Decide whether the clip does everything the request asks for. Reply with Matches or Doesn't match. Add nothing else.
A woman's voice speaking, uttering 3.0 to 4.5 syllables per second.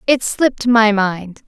Matches